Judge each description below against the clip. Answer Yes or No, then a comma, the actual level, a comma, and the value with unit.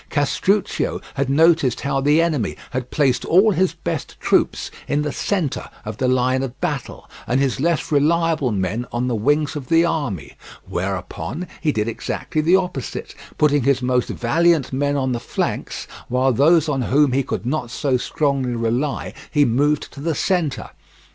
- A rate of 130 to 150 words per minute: No, average, 170 wpm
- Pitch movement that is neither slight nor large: Yes, average, 3.8 semitones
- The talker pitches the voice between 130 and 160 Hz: Yes, medium, 140 Hz